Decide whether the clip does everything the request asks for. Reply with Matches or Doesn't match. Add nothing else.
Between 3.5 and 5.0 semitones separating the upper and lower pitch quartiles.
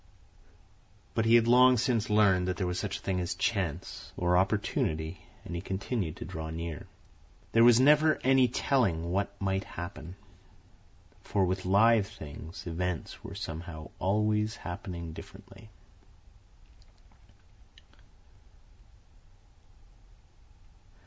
Matches